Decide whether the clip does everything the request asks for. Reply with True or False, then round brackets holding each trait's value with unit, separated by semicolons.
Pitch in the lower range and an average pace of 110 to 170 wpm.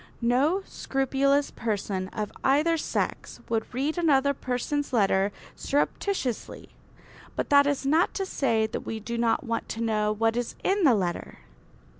False (255 Hz; 150 wpm)